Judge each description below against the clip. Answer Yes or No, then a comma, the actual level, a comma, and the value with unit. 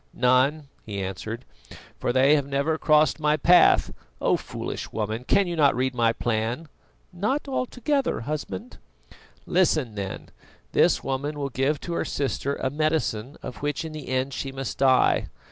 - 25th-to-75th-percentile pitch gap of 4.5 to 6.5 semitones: No, average, 3.7 semitones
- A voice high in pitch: No, medium, 140 Hz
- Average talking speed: Yes, average, 155 wpm